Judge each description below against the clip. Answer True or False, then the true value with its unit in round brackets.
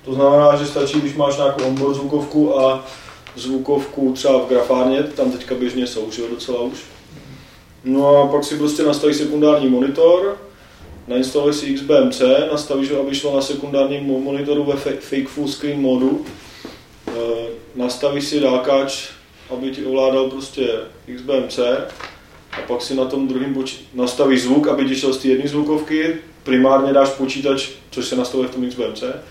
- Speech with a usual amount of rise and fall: False (1.8 semitones)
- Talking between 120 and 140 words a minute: False (160 wpm)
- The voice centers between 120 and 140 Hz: True (135 Hz)